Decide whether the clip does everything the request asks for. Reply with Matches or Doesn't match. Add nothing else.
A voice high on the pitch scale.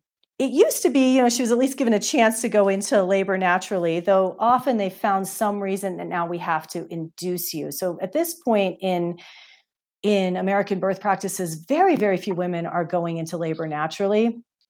Matches